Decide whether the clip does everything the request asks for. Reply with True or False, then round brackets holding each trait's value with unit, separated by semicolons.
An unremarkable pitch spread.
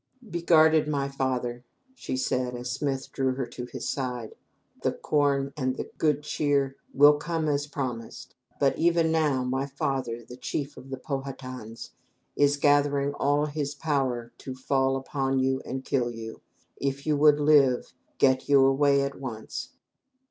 False (2.0 semitones)